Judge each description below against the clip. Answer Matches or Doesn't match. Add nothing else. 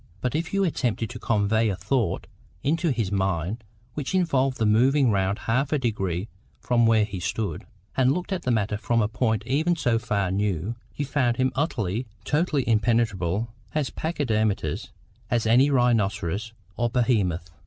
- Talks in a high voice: Doesn't match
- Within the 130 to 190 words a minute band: Matches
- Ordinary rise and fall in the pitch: Matches